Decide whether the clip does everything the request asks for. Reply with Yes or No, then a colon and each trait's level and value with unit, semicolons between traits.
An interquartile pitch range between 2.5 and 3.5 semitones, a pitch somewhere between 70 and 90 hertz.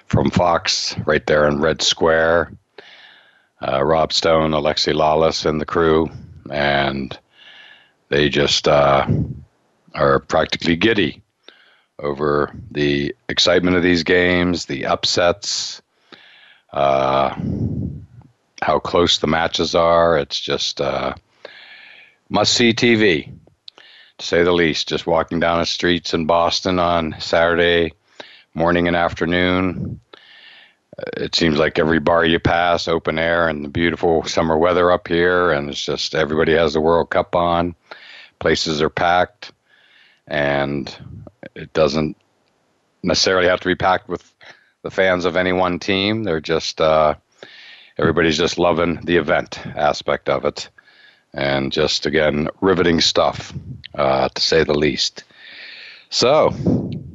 Yes: average, 2.8 semitones; very low, 85 Hz